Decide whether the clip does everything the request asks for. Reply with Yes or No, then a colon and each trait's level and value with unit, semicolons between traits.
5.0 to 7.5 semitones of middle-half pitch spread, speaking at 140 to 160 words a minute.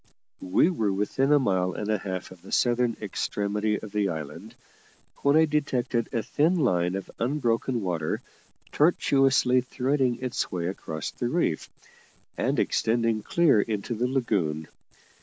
Yes: wide, 5.4 semitones; average, 145 wpm